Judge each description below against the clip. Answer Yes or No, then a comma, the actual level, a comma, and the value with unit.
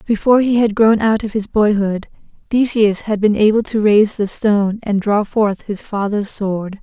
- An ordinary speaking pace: Yes, average, 195 wpm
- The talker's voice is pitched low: No, high, 210 Hz